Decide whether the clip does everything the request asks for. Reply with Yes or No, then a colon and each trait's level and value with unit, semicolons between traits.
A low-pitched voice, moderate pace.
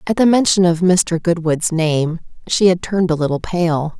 No: medium, 170 Hz; average, 195 wpm